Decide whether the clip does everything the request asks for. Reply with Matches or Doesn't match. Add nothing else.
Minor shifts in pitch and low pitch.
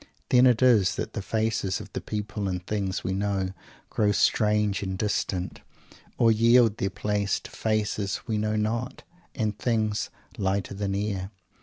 Matches